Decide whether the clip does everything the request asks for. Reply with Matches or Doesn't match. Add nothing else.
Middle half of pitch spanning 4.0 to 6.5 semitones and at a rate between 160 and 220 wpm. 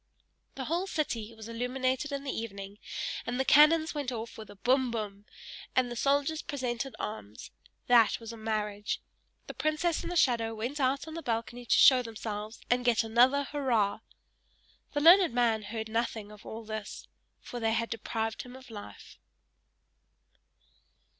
Doesn't match